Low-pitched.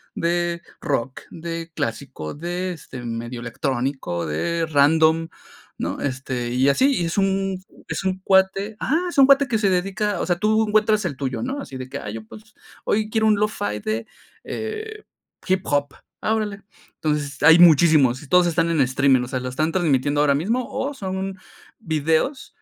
No: medium, 170 Hz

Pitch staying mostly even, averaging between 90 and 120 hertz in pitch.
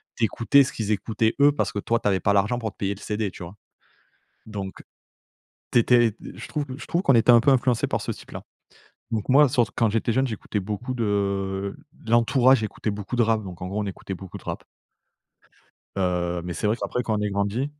No: average, 3.5 semitones; low, 110 Hz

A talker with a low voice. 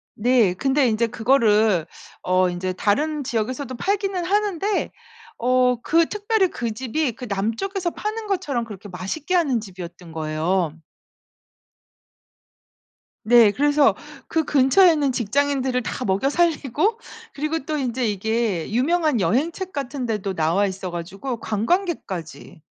No: very high, 250 Hz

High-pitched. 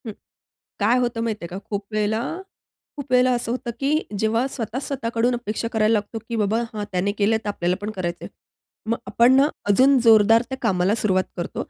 Yes: high, 225 Hz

